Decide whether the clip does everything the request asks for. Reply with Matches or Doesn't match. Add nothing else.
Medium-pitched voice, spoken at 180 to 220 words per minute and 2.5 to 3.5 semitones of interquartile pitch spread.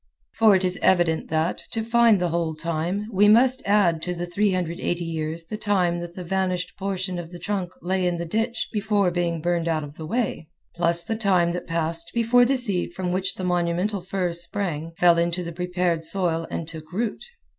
Matches